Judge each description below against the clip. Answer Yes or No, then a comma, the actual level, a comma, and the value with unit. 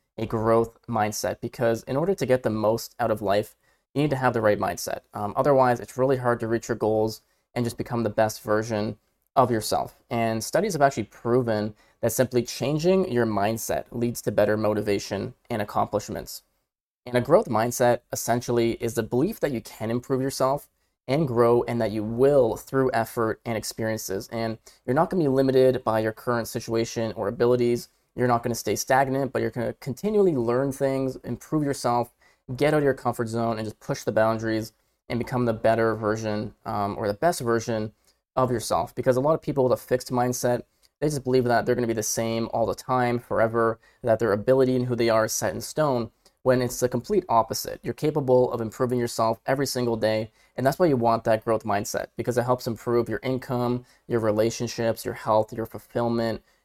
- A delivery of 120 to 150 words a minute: No, average, 200 wpm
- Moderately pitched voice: No, low, 120 Hz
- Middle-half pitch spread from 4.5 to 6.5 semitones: No, narrow, 2.4 semitones